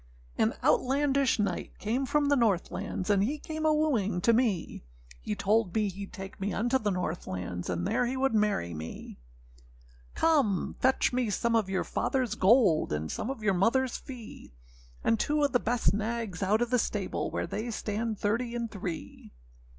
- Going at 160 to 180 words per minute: No, average, 190 wpm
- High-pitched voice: Yes, high, 220 Hz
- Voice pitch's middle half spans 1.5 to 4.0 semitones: No, average, 4.6 semitones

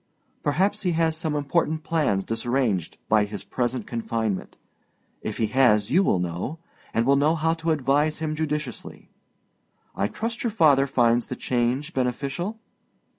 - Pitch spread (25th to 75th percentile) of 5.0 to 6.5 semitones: Yes, wide, 5.4 semitones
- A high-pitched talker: No, medium, 140 Hz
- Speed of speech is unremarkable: Yes, average, 150 wpm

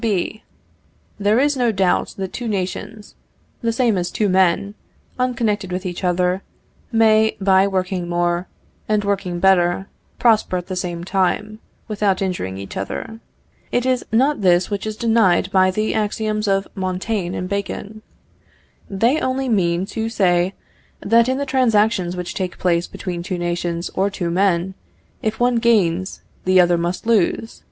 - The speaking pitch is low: No, high, 195 Hz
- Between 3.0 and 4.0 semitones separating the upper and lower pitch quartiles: Yes, average, 3.5 semitones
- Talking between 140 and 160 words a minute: Yes, average, 155 wpm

